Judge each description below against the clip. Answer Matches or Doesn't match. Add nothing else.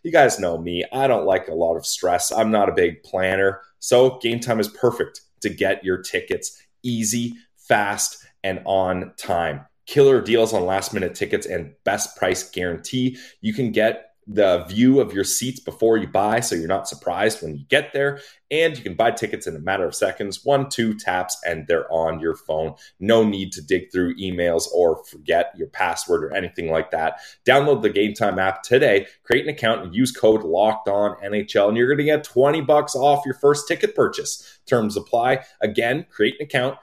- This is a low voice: Matches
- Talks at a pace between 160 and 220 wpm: Matches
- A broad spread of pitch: Matches